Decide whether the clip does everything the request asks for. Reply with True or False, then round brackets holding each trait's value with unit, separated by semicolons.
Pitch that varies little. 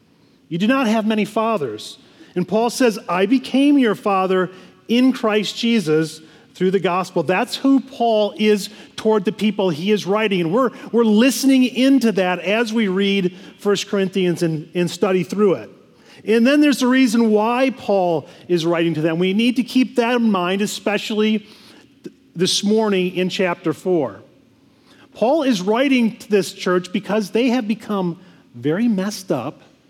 False (4.1 semitones)